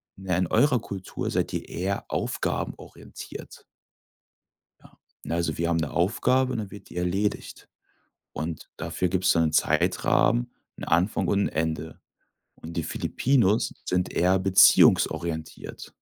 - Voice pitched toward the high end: No, very low, 90 Hz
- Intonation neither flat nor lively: Yes, average, 3.1 semitones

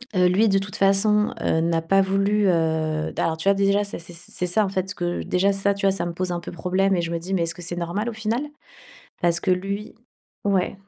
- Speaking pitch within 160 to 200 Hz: Yes, medium, 185 Hz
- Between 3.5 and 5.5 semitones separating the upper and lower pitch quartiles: No, narrow, 2.5 semitones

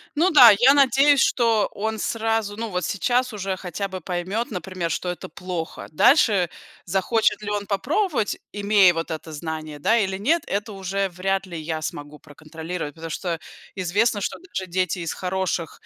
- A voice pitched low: No, high, 190 Hz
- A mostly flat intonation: No, average, 4.3 semitones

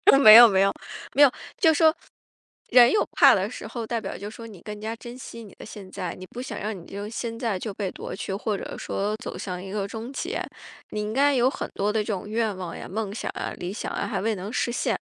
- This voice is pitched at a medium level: No, high, 215 Hz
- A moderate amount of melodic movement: Yes, average, 3.2 semitones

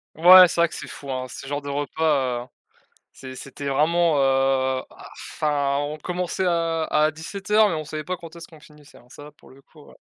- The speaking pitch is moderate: Yes, medium, 150 Hz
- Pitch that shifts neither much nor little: Yes, average, 3.4 semitones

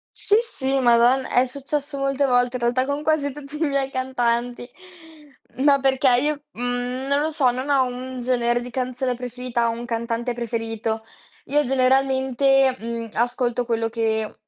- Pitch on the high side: Yes, very high, 255 Hz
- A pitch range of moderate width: No, narrow, 2.2 semitones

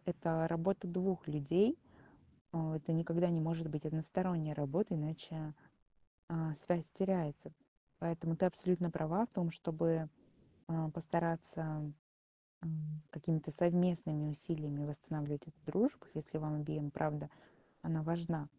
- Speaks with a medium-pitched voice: Yes, medium, 160 Hz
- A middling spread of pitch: No, narrow, 1.9 semitones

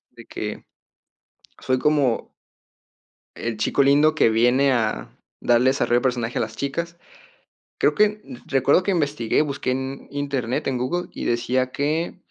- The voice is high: No, low, 135 Hz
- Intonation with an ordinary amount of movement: Yes, average, 3.3 semitones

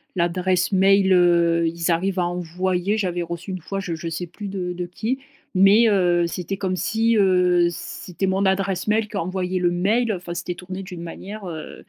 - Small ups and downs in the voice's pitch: Yes, narrow, 2.1 semitones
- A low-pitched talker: No, medium, 185 Hz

